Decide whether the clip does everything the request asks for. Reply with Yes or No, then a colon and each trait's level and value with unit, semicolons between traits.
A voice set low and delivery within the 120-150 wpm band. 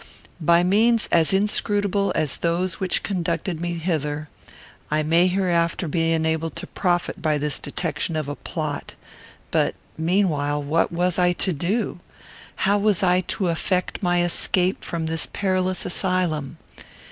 No: medium, 175 Hz; average, 145 wpm